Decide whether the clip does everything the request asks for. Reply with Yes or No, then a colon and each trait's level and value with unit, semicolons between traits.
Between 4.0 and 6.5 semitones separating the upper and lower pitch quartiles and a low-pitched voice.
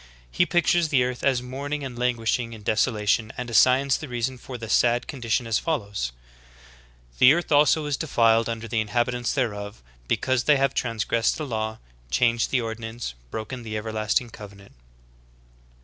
No: average, 2.9 semitones; low, 120 Hz